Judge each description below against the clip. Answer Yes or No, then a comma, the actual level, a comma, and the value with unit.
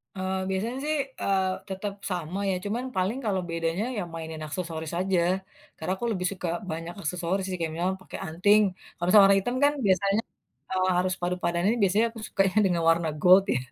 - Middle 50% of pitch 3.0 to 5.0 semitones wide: No, narrow, 2.4 semitones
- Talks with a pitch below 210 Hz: Yes, medium, 185 Hz